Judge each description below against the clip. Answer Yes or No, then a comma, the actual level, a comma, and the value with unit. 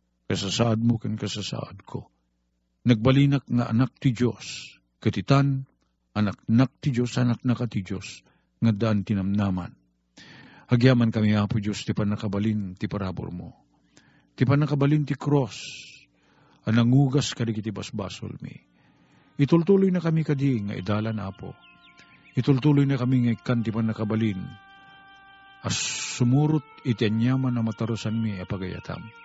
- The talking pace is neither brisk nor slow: Yes, average, 125 wpm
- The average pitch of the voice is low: Yes, low, 115 Hz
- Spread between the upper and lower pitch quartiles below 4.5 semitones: No, average, 4.9 semitones